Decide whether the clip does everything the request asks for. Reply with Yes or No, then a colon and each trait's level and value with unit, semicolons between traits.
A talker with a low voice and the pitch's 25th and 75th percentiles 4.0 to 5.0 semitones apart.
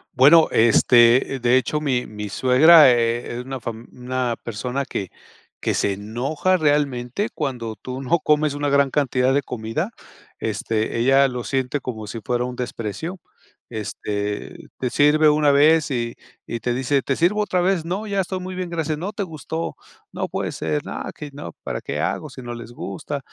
Yes: low, 130 Hz; average, 4.4 semitones